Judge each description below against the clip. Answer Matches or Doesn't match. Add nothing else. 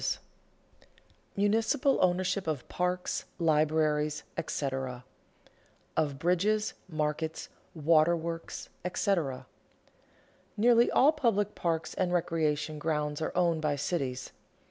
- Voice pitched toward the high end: Doesn't match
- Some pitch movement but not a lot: Matches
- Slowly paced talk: Matches